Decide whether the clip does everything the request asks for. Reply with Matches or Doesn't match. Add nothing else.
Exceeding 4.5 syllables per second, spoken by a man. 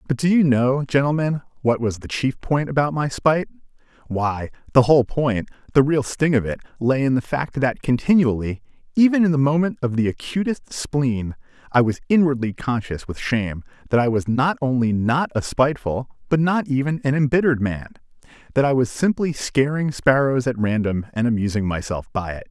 Matches